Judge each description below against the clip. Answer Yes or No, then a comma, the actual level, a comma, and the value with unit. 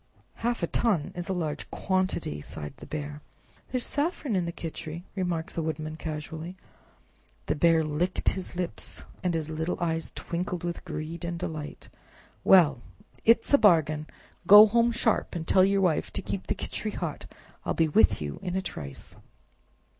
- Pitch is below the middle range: No, medium, 170 Hz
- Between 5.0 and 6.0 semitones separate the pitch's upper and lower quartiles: No, average, 3.4 semitones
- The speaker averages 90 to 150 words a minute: No, average, 170 wpm